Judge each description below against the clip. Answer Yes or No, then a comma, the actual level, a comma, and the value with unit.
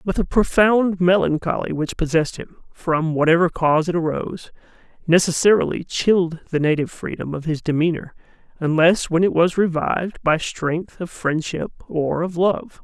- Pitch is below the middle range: No, medium, 170 Hz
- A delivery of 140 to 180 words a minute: Yes, average, 150 wpm